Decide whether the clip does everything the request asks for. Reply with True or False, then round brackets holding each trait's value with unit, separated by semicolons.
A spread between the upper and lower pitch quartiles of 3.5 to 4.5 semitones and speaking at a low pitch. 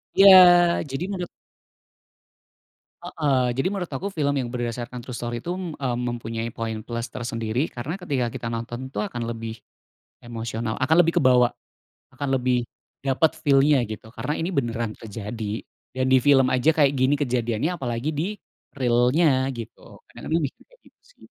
True (3.8 semitones; 125 Hz)